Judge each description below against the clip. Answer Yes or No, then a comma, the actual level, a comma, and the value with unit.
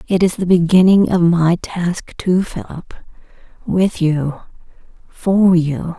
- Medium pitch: Yes, medium, 170 Hz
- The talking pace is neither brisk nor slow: No, slow, 120 wpm